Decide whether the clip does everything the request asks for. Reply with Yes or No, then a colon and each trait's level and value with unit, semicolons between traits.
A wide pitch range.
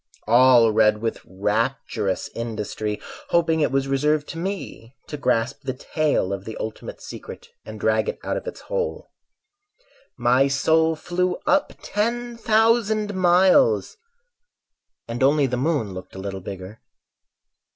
Yes: wide, 8.3 semitones